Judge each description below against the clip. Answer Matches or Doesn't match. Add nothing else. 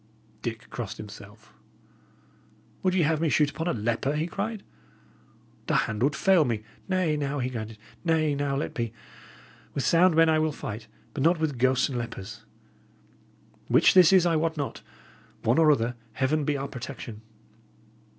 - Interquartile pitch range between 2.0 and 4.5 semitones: Doesn't match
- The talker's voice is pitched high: Doesn't match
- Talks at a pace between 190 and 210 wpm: Doesn't match